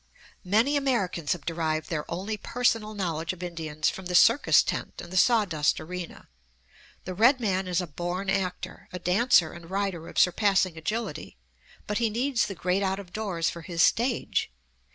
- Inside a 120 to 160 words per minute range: No, average, 175 wpm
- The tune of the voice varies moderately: Yes, average, 3.9 semitones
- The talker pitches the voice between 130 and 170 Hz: No, medium, 185 Hz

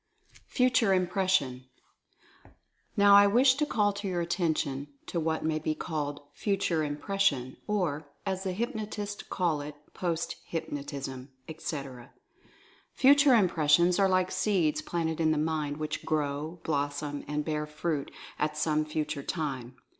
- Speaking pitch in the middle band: Yes, medium, 160 Hz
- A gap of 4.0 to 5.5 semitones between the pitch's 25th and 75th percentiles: Yes, average, 4.5 semitones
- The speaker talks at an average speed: No, slow, 130 wpm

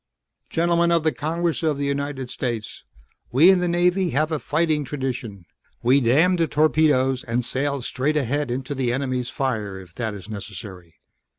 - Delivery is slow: No, average, 170 wpm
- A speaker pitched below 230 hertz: Yes, medium, 140 Hz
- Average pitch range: Yes, average, 4.5 semitones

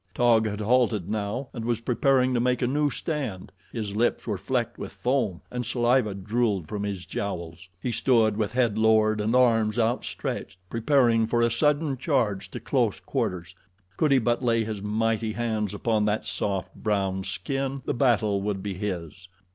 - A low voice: Yes, low, 110 Hz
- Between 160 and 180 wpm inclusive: Yes, average, 175 wpm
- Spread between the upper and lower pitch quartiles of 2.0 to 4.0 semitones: Yes, average, 3.2 semitones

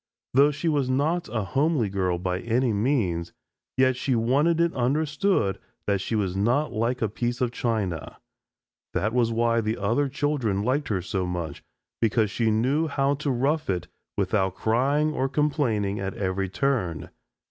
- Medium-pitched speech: No, low, 120 Hz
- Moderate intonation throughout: No, wide, 5.9 semitones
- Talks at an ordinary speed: Yes, average, 165 wpm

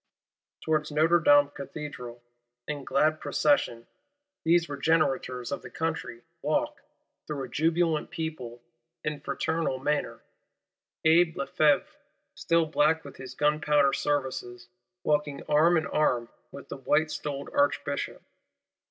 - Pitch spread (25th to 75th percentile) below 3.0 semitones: Yes, narrow, 2.5 semitones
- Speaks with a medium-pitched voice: Yes, medium, 150 Hz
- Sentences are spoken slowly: Yes, slow, 120 wpm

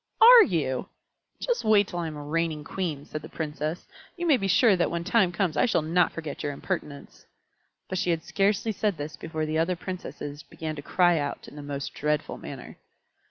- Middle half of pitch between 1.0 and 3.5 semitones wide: No, average, 4.2 semitones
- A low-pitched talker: No, medium, 165 Hz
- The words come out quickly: Yes, fast, 215 wpm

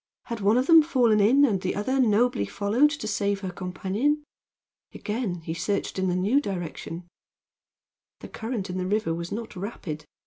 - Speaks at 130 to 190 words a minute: Yes, average, 175 wpm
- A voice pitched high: Yes, high, 205 Hz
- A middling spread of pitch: Yes, average, 5.0 semitones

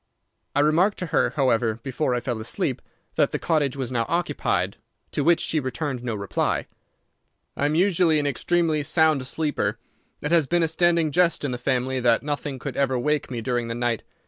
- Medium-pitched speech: Yes, medium, 145 Hz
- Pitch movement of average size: Yes, average, 4.4 semitones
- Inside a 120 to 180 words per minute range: No, average, 195 wpm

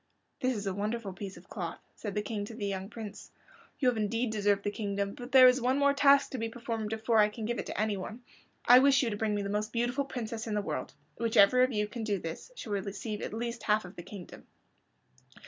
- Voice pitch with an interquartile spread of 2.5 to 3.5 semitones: Yes, average, 2.9 semitones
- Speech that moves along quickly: Yes, fast, 255 wpm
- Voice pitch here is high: Yes, high, 220 Hz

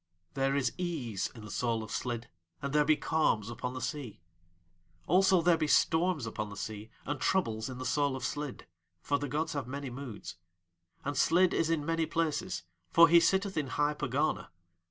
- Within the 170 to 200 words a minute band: Yes, average, 190 wpm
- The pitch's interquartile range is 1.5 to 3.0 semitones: No, average, 5.0 semitones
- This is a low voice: No, medium, 145 Hz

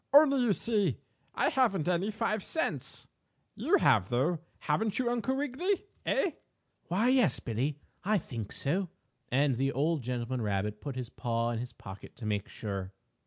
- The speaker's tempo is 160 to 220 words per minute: Yes, average, 165 wpm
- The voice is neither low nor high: Yes, medium, 150 Hz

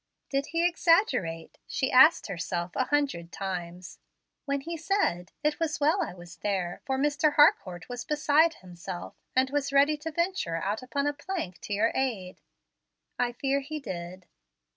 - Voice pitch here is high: Yes, very high, 265 Hz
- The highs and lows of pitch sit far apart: Yes, wide, 8.7 semitones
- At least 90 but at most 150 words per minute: No, average, 165 wpm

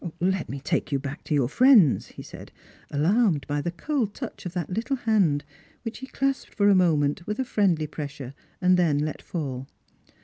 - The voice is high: No, medium, 175 Hz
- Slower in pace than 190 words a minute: No, average, 200 wpm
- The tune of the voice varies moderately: No, wide, 6.5 semitones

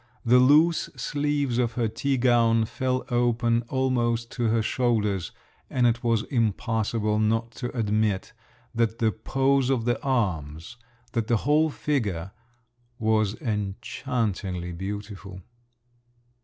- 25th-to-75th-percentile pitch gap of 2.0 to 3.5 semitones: Yes, average, 3.1 semitones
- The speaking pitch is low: Yes, low, 115 Hz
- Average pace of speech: No, slow, 120 wpm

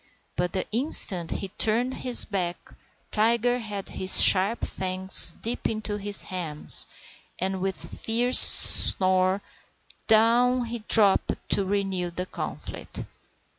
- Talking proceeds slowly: Yes, slow, 125 wpm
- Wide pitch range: No, average, 3.6 semitones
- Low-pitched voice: No, high, 200 Hz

